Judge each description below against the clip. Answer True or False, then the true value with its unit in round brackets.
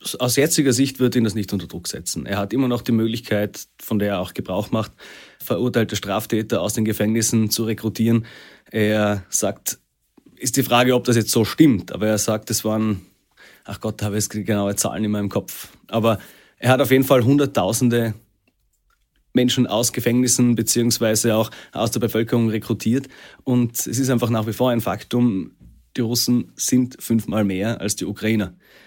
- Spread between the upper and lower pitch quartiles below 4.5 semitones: True (2.5 semitones)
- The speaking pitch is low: True (115 Hz)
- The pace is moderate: True (180 wpm)